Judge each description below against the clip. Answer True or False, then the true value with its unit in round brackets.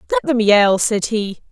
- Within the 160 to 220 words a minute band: True (200 wpm)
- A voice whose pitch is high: True (220 Hz)